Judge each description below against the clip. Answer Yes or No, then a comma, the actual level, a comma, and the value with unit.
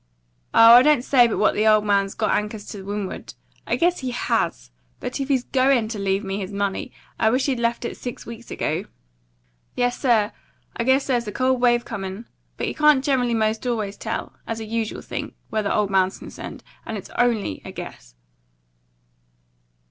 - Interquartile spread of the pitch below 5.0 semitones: Yes, average, 3.3 semitones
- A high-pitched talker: Yes, high, 225 Hz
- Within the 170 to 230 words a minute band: Yes, average, 190 wpm